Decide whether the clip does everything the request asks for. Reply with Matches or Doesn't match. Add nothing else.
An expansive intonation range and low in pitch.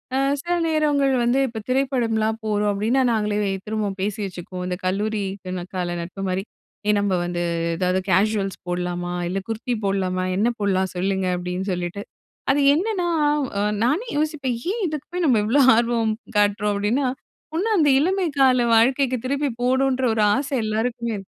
Doesn't match